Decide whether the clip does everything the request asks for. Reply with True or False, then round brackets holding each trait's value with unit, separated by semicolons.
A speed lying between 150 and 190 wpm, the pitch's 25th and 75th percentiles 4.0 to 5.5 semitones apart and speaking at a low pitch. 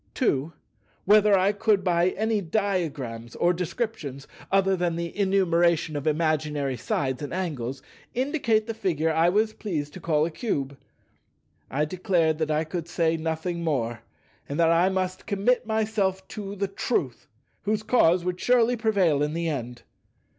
False (155 wpm; 4.7 semitones; 175 Hz)